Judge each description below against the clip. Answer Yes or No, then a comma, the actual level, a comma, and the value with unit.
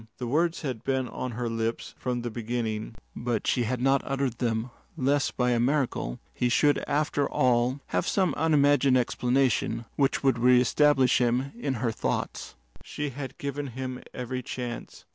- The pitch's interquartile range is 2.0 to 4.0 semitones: Yes, narrow, 2.5 semitones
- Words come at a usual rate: Yes, average, 160 wpm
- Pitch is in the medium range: No, low, 125 Hz